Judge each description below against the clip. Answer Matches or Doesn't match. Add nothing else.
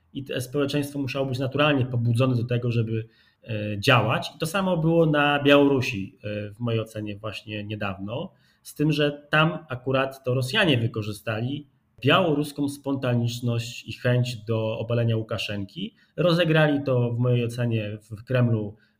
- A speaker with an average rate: Matches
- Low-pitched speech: Matches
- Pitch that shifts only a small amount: Doesn't match